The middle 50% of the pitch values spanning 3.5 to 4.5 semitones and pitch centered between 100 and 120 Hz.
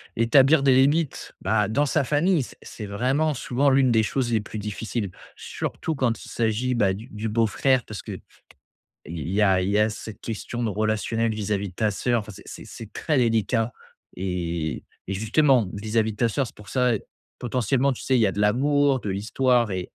Yes: average, 3.9 semitones; low, 115 Hz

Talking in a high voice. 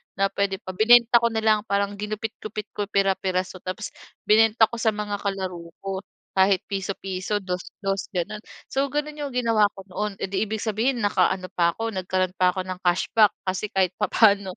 Yes: high, 200 Hz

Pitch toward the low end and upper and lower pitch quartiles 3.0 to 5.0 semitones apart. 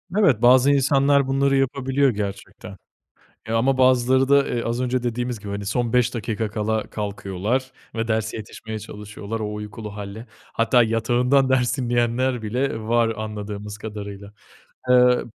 Yes: low, 115 Hz; average, 3.4 semitones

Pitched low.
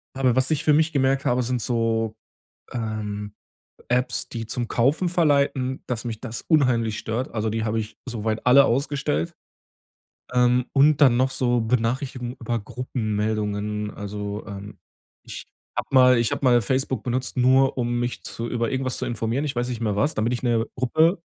Yes: low, 120 Hz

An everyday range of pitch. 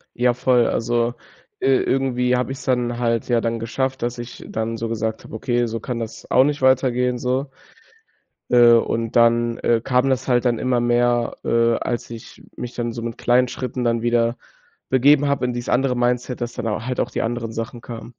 No: narrow, 1.4 semitones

